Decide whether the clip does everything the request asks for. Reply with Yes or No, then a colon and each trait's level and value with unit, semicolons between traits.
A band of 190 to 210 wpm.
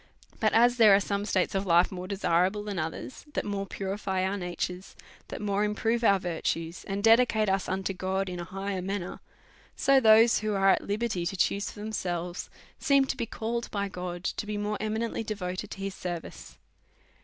Yes: average, 195 wpm